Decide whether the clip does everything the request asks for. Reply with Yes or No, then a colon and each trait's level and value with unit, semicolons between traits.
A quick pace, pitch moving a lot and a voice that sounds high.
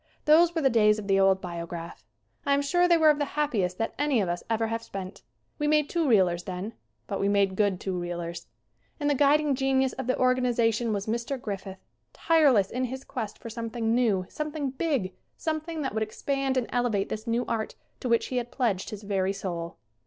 Yes: fast, 215 wpm; wide, 5.9 semitones; high, 230 Hz